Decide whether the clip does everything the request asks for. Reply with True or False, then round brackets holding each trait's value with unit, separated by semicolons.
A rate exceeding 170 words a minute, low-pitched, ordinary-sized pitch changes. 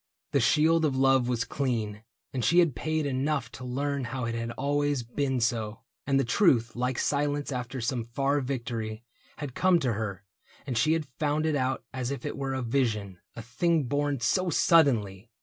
True (190 wpm; 130 Hz; 3.7 semitones)